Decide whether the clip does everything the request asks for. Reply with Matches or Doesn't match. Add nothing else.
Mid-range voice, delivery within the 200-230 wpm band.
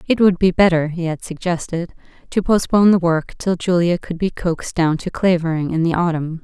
Matches